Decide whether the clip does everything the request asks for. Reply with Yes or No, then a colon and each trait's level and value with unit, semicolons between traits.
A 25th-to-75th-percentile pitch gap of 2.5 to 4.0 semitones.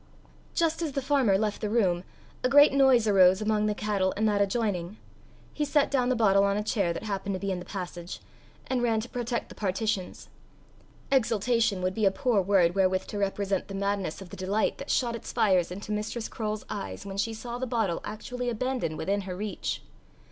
Yes: average, 3.6 semitones